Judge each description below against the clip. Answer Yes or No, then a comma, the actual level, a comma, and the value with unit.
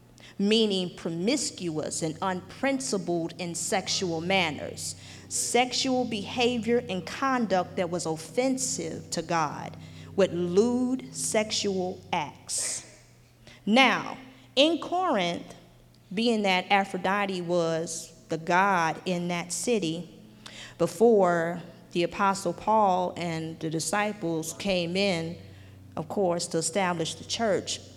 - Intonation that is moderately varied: Yes, average, 4.5 semitones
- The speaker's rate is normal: No, slow, 100 wpm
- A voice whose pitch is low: No, medium, 180 Hz